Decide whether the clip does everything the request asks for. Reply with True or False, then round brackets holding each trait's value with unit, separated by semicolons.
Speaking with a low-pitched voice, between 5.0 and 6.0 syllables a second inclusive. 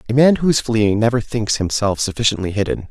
True (115 Hz; 5.9 syllables/s)